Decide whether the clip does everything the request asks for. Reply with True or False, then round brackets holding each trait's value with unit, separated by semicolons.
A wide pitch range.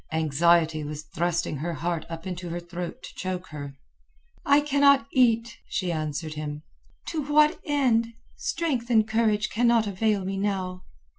True (6.2 semitones)